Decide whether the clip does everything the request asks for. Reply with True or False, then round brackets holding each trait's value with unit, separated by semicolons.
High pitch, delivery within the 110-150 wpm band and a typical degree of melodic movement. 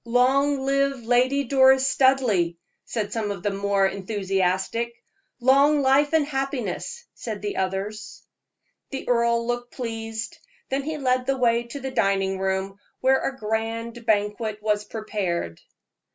True (235 Hz; 140 wpm; 4.6 semitones)